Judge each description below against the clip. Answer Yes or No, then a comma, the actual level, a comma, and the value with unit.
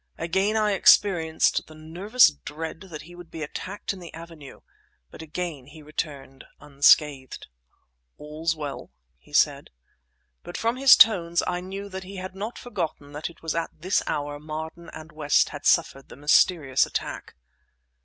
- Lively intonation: No, average, 3.8 semitones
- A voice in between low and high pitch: Yes, medium, 165 Hz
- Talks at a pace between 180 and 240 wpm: No, average, 155 wpm